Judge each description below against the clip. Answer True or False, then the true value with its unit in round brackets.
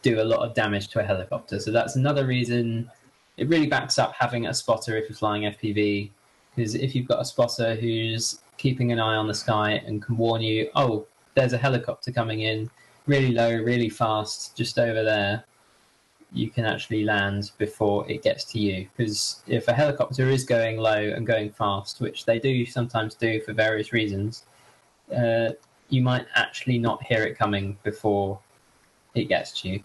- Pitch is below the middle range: True (115 Hz)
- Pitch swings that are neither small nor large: False (2.3 semitones)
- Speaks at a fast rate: False (185 wpm)